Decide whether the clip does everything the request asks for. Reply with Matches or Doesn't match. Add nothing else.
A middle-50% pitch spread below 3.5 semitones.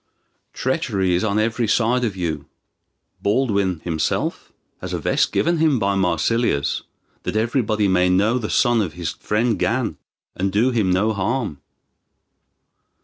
Doesn't match